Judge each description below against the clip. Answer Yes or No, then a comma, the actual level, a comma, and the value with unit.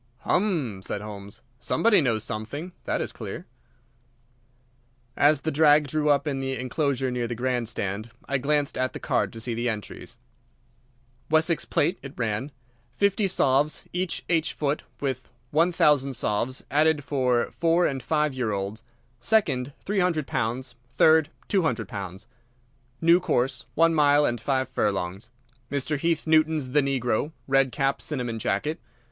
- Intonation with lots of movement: No, average, 4.4 semitones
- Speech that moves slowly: No, average, 145 wpm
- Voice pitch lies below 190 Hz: Yes, low, 135 Hz